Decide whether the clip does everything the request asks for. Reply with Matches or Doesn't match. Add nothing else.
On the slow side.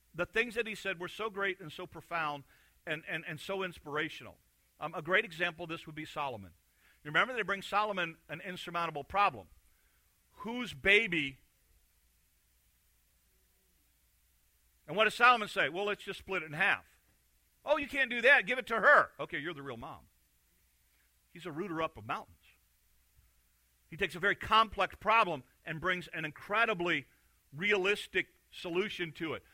Doesn't match